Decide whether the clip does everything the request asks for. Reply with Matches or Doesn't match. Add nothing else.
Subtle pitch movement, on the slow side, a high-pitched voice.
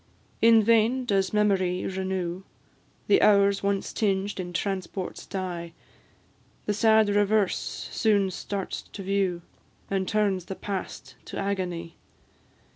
Matches